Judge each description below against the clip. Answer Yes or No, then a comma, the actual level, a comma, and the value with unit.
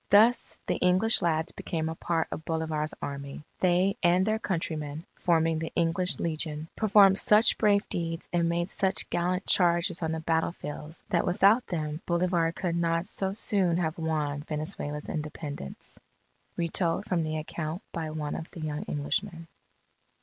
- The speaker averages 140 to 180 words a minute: Yes, average, 155 wpm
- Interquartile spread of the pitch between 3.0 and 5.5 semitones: No, narrow, 2.5 semitones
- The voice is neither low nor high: Yes, medium, 165 Hz